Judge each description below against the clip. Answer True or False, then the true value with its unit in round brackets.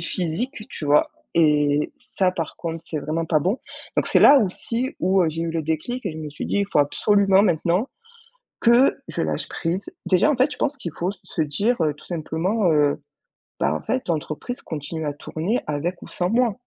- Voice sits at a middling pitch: True (170 Hz)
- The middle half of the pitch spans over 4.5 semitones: True (5.1 semitones)